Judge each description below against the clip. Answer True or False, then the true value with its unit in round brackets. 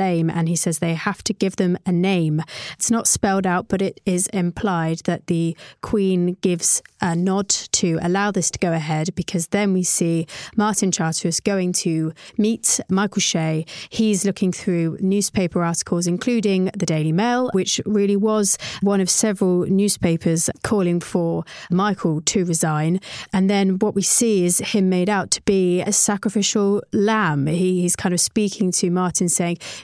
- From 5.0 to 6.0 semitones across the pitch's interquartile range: False (2.8 semitones)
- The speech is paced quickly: False (170 wpm)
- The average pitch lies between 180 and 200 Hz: True (185 Hz)